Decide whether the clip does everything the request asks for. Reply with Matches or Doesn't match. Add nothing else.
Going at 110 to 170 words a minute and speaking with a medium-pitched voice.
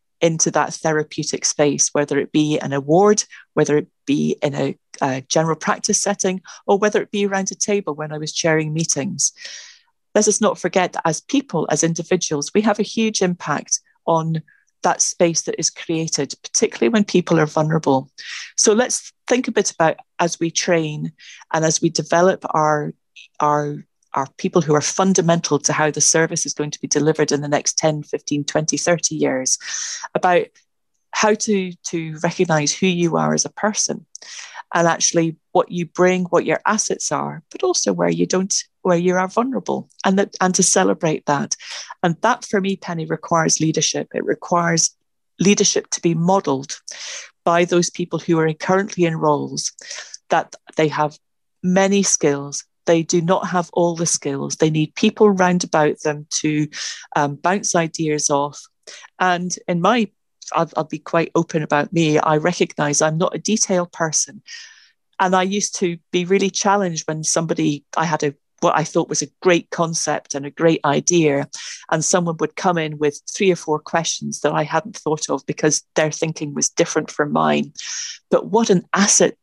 Doesn't match